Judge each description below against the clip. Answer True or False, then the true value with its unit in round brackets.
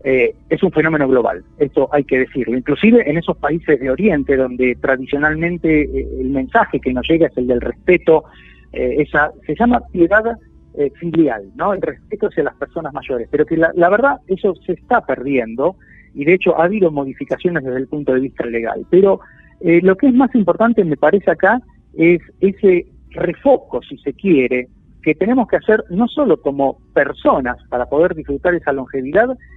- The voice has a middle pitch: True (160 Hz)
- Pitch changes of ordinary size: False (6.0 semitones)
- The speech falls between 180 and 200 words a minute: True (185 wpm)